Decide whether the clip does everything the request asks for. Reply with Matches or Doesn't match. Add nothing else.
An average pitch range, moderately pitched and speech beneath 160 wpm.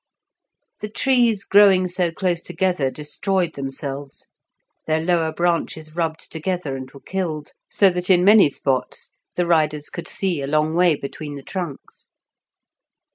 Matches